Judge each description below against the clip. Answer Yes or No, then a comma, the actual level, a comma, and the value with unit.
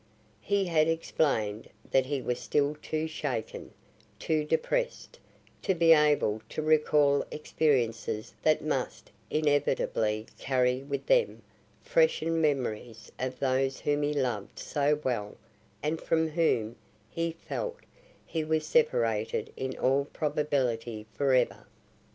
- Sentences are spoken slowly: Yes, slow, 120 wpm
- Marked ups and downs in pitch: No, average, 4.1 semitones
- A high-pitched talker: No, medium, 145 Hz